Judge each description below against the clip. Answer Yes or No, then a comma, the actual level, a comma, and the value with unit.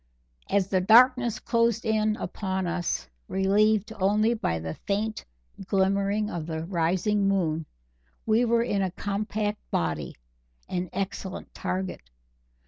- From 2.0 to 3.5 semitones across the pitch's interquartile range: Yes, average, 3.0 semitones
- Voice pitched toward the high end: Yes, high, 195 Hz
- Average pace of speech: No, slow, 125 wpm